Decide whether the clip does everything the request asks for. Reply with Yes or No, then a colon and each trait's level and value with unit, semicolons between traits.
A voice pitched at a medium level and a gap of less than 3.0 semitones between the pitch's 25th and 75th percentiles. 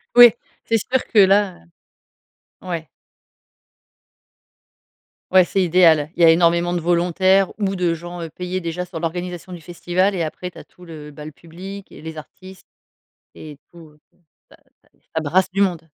Yes: medium, 175 Hz; narrow, 2.4 semitones